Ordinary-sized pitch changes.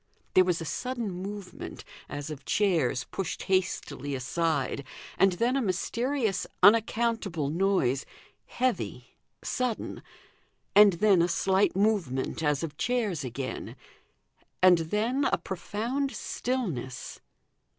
No: wide, 6.2 semitones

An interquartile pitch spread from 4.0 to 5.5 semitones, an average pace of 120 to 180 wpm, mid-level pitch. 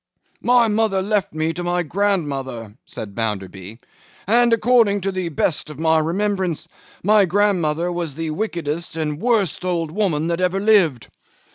Yes: average, 4.9 semitones; average, 155 wpm; medium, 175 Hz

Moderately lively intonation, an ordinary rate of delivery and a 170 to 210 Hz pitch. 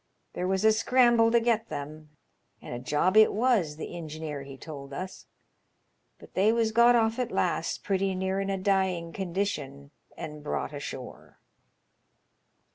No: wide, 6.5 semitones; average, 155 wpm; high, 190 Hz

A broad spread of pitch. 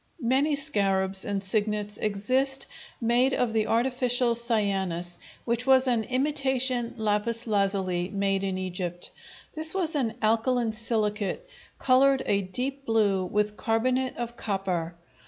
No: average, 4.4 semitones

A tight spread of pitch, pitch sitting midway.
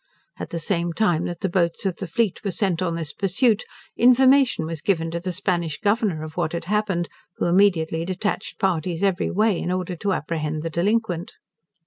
No: average, 3.4 semitones; medium, 180 Hz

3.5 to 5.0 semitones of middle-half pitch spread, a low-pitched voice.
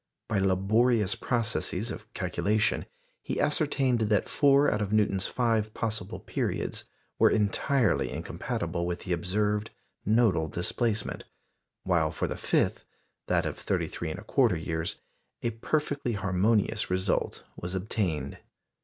Yes: average, 3.9 semitones; low, 105 Hz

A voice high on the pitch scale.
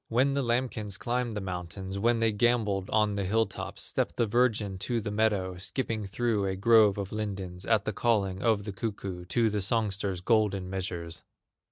No: low, 105 Hz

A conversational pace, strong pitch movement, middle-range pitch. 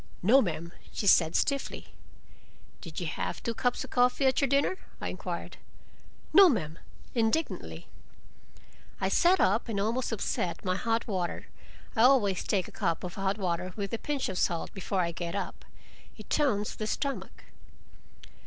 No: average, 160 wpm; wide, 5.9 semitones; high, 210 Hz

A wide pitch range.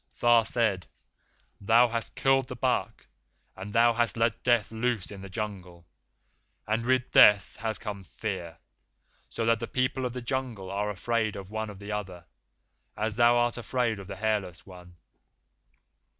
No: average, 3.2 semitones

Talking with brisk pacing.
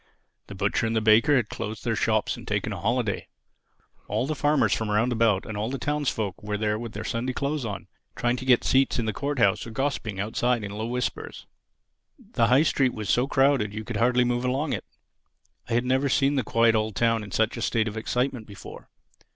Yes: fast, 220 wpm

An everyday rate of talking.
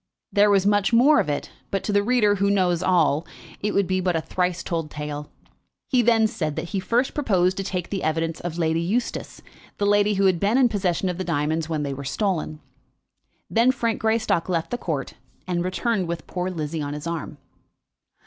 No: fast, 210 wpm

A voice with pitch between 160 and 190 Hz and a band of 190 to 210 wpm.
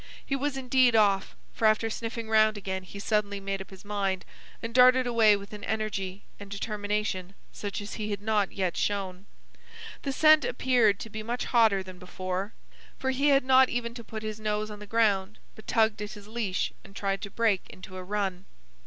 No: high, 210 Hz; average, 200 wpm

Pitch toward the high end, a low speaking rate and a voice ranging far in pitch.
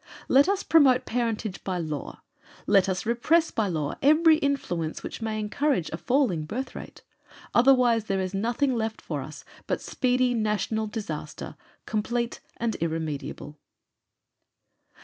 Yes: high, 220 Hz; slow, 130 wpm; wide, 5.9 semitones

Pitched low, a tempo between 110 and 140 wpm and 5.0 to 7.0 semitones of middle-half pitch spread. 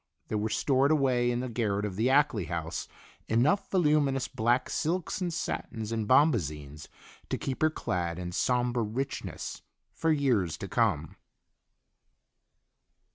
Yes: low, 120 Hz; slow, 135 wpm; wide, 5.4 semitones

